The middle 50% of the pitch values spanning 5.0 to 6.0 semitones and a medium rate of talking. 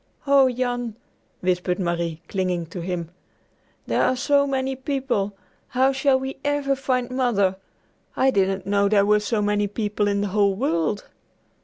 Yes: wide, 5.4 semitones; average, 155 wpm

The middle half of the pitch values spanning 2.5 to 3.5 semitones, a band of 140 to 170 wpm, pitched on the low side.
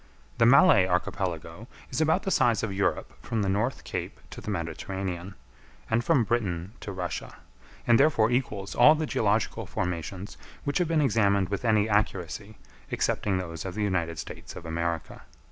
No: average, 4.6 semitones; average, 165 wpm; low, 100 Hz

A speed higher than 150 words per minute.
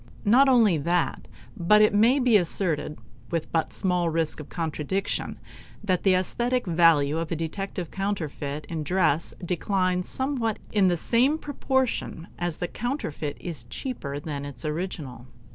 No: average, 145 wpm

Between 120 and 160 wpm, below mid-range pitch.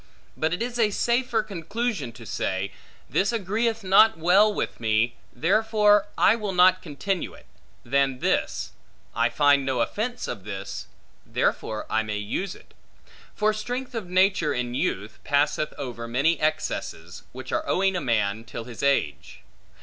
No: average, 155 wpm; medium, 160 Hz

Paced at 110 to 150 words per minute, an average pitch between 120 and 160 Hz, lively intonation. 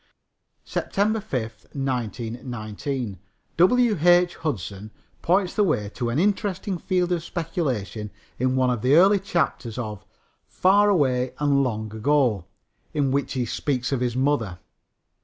Yes: slow, 135 wpm; low, 135 Hz; wide, 7.1 semitones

